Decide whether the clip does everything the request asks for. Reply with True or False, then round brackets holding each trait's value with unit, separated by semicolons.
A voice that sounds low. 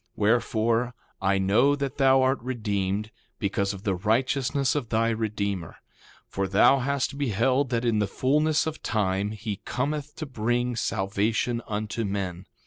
True (115 Hz)